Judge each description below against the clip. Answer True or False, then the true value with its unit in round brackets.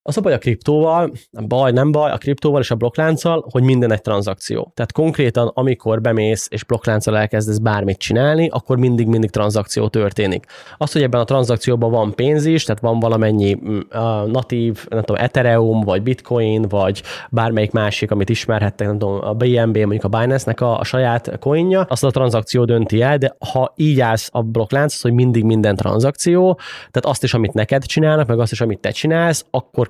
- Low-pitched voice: True (120 Hz)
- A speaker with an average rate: False (185 wpm)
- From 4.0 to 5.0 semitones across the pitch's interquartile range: False (3.5 semitones)